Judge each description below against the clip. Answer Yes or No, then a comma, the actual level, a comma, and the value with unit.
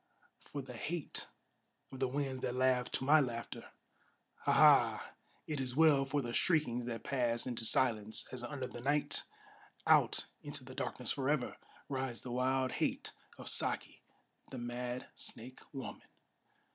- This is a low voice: Yes, low, 130 Hz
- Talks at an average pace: Yes, average, 150 wpm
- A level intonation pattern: Yes, narrow, 2.1 semitones